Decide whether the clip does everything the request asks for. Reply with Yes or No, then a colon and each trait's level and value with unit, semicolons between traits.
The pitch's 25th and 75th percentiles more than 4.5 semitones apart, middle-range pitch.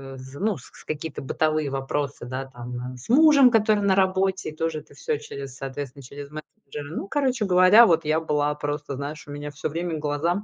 Yes: average, 5.0 semitones; medium, 150 Hz